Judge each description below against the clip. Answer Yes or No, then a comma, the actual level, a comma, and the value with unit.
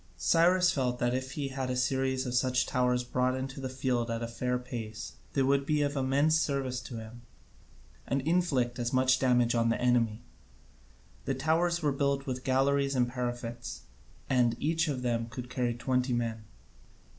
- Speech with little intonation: Yes, narrow, 2.2 semitones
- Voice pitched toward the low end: Yes, low, 130 Hz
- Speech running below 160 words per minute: No, average, 175 wpm